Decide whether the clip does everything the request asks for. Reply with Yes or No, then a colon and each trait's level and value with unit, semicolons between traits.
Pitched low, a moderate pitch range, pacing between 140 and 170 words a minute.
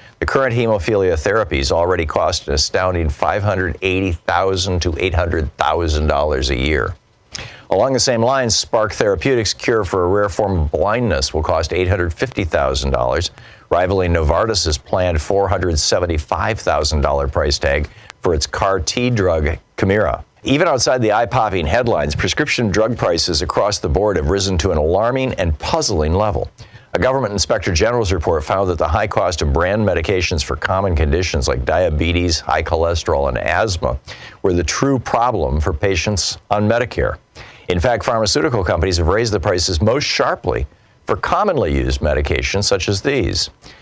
Yes: very low, 90 Hz; average, 4.3 semitones; average, 150 wpm